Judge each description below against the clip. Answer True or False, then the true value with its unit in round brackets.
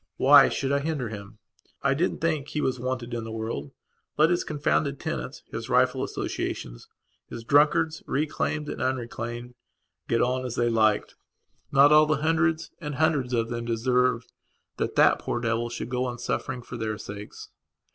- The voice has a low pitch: True (125 Hz)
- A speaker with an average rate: True (170 wpm)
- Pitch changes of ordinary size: True (4.0 semitones)